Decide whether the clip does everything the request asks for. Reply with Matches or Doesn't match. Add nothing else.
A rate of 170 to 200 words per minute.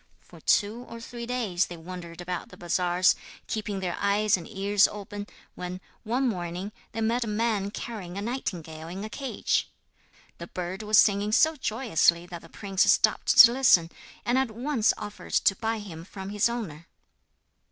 Matches